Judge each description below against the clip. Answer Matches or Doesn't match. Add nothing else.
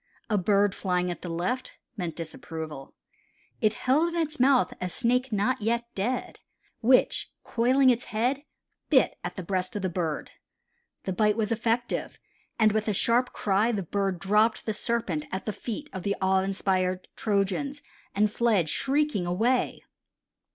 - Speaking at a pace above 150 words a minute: Matches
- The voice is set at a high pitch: Matches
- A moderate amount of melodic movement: Matches